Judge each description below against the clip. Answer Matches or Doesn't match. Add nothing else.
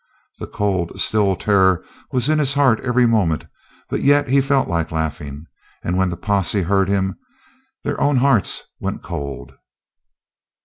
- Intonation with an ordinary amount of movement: Doesn't match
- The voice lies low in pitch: Matches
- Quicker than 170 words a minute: Doesn't match